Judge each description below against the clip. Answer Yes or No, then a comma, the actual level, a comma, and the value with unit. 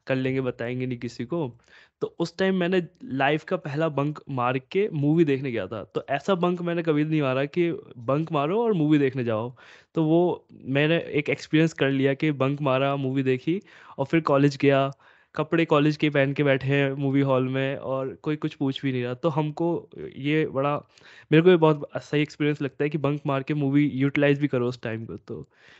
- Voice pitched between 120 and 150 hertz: Yes, medium, 140 Hz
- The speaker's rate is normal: No, fast, 210 wpm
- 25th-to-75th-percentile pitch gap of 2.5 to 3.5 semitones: Yes, average, 2.8 semitones